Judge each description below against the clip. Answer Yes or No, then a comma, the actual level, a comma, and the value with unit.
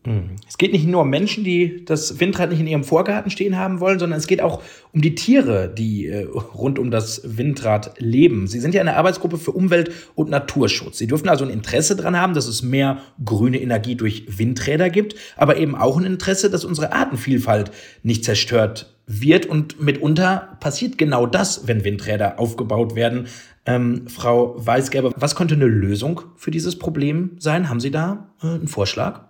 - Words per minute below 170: No, average, 180 wpm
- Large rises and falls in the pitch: Yes, wide, 6.9 semitones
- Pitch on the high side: No, medium, 140 Hz